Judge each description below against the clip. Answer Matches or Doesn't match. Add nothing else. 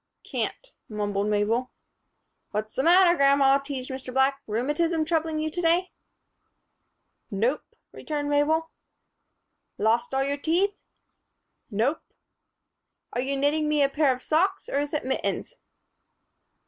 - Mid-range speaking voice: Doesn't match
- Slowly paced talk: Matches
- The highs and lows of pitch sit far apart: Doesn't match